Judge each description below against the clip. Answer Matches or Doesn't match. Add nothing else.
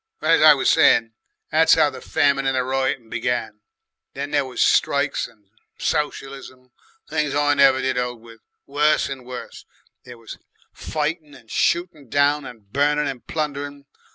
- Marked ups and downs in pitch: Doesn't match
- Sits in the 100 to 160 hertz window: Matches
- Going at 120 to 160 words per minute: Matches